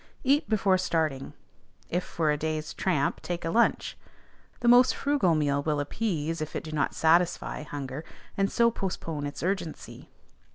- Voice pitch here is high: No, medium, 165 Hz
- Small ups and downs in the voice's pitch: No, average, 4.6 semitones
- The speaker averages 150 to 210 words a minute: Yes, average, 160 wpm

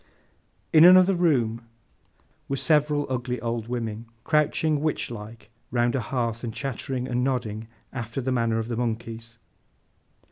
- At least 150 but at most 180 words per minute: No, average, 140 wpm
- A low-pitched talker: Yes, low, 120 Hz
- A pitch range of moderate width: Yes, average, 3.2 semitones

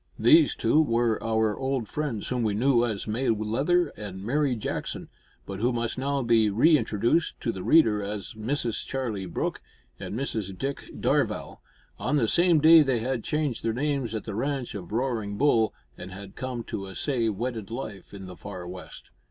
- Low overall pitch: Yes, low, 115 Hz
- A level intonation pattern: No, average, 4.5 semitones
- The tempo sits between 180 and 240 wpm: Yes, average, 185 wpm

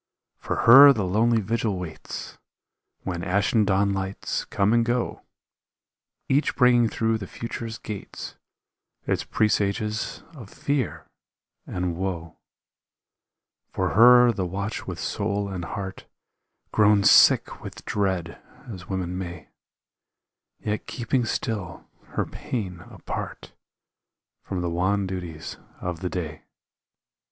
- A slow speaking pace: Yes, slow, 115 wpm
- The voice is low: Yes, low, 100 Hz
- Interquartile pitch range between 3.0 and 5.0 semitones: Yes, average, 3.8 semitones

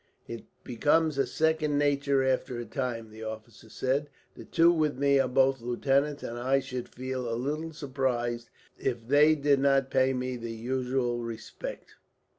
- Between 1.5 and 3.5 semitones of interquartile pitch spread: Yes, average, 2.9 semitones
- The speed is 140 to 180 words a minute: Yes, average, 165 wpm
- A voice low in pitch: Yes, low, 130 Hz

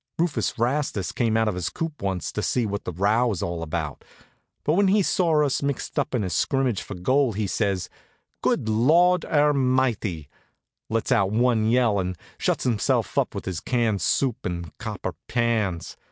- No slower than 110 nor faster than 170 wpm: No, average, 180 wpm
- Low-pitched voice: Yes, low, 115 Hz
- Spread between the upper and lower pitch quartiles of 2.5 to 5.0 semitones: No, wide, 5.6 semitones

